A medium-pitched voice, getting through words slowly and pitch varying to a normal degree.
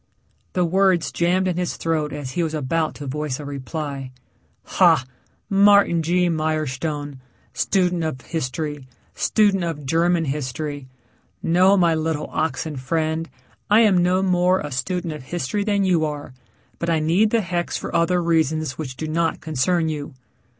No: medium, 160 Hz; average, 155 wpm; average, 3.3 semitones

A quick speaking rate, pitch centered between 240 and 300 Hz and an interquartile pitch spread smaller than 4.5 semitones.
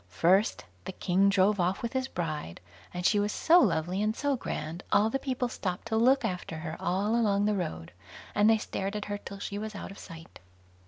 No: fast, 215 wpm; high, 200 Hz; average, 3.7 semitones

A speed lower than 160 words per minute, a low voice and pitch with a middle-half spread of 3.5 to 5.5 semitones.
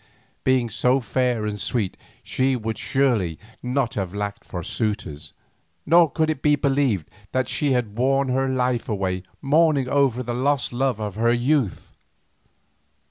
Yes: average, 150 wpm; low, 125 Hz; average, 4.2 semitones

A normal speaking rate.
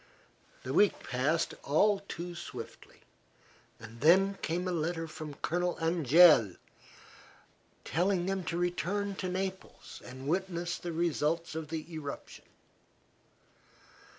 No: slow, 115 wpm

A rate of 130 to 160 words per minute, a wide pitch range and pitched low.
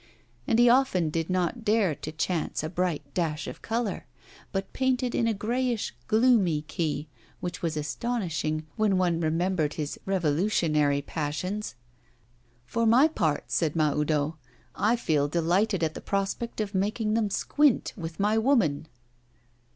No: average, 145 wpm; wide, 6.0 semitones; medium, 180 Hz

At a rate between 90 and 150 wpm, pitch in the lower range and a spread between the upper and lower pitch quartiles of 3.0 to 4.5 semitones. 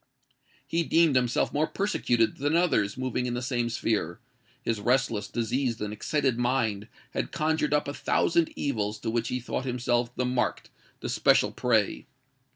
No: average, 160 wpm; low, 125 Hz; average, 3.8 semitones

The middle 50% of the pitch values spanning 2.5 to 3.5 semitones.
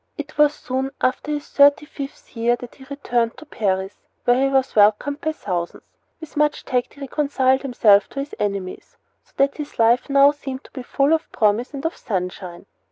No: average, 4.0 semitones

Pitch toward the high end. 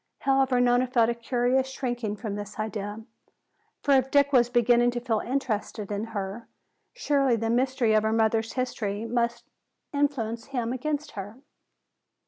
Yes: high, 240 Hz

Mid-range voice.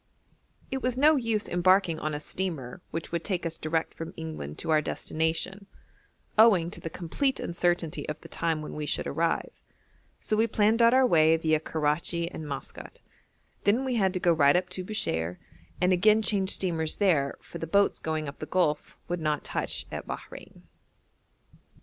Yes: medium, 170 Hz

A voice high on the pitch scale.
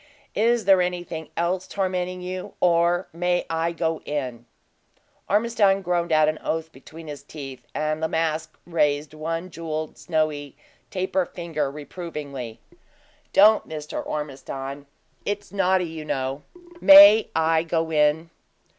No: medium, 165 Hz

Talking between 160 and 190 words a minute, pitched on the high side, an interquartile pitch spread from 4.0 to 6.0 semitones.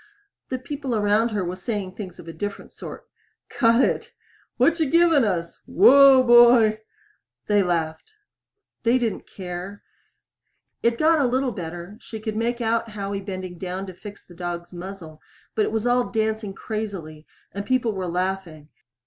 Yes: average, 165 wpm; high, 205 Hz; average, 4.6 semitones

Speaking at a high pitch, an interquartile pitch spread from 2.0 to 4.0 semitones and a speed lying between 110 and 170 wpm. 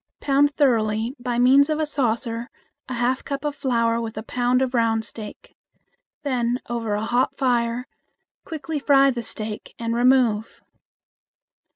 Yes: high, 245 Hz; average, 2.9 semitones; average, 150 wpm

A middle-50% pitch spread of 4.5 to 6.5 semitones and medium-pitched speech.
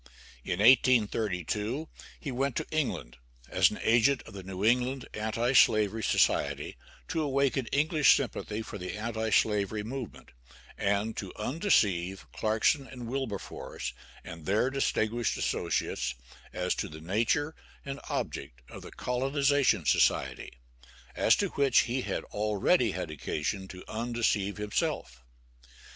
No: average, 4.9 semitones; low, 110 Hz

